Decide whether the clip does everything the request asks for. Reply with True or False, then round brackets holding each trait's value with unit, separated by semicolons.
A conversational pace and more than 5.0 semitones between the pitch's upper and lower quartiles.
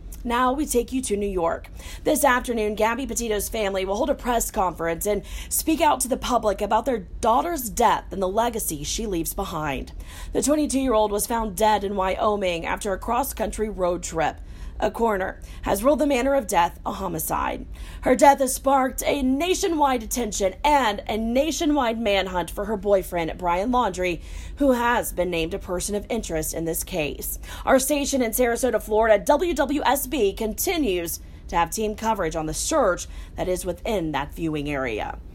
True (180 wpm; 5.6 semitones)